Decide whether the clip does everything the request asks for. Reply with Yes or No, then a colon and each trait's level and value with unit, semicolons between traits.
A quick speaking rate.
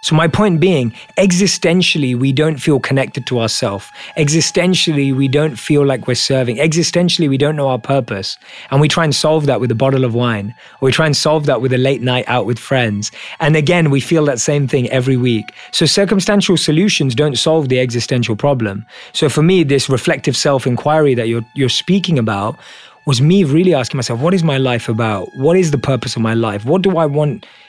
Yes: fast, 210 wpm